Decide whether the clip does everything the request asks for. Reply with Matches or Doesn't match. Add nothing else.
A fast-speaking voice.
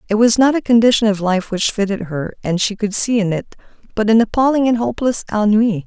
Matches